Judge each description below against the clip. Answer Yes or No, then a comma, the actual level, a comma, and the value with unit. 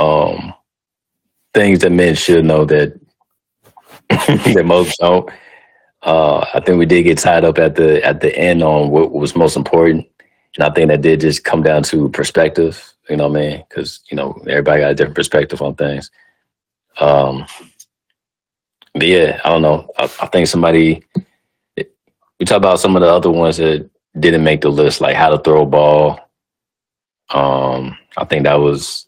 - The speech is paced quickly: No, average, 180 wpm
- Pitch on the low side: Yes, very low, 75 Hz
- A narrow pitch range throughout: Yes, narrow, 1.9 semitones